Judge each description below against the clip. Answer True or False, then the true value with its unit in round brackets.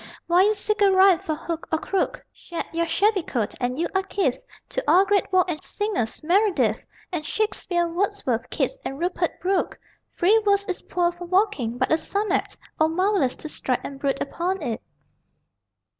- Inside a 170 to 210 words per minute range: True (180 wpm)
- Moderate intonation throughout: True (4.3 semitones)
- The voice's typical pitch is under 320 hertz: False (355 Hz)